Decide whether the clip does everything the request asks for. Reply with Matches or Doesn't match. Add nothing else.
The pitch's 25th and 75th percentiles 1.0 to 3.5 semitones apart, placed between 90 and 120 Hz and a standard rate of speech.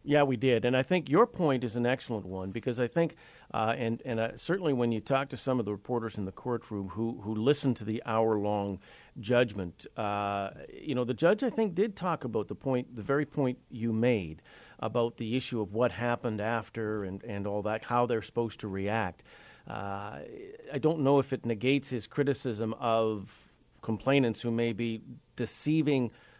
Matches